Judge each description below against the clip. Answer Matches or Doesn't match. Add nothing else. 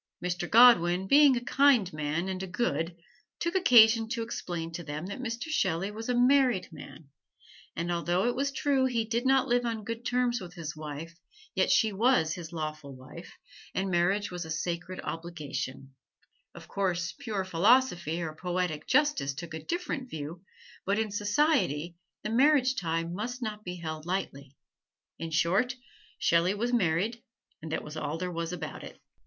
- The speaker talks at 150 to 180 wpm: Matches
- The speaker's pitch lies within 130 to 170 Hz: Doesn't match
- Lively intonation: Matches